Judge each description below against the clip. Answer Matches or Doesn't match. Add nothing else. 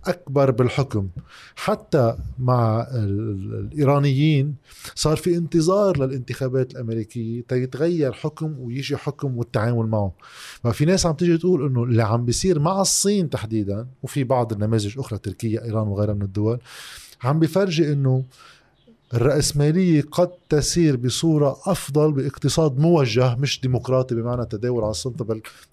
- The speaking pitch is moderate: Doesn't match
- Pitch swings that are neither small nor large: Matches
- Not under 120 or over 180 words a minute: Matches